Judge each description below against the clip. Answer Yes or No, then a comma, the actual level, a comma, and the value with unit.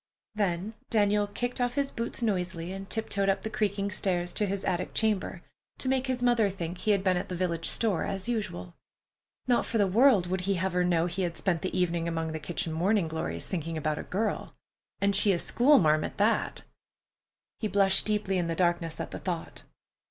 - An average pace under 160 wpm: No, fast, 205 wpm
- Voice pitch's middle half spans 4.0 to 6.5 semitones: No, average, 3.5 semitones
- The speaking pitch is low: No, high, 190 Hz